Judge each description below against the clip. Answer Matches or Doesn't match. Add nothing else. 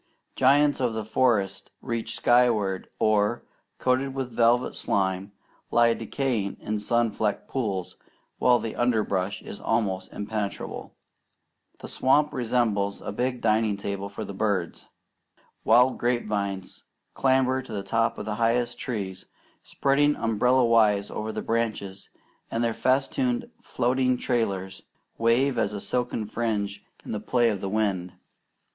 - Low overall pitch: Matches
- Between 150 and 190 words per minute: Doesn't match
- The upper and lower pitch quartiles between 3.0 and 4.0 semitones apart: Matches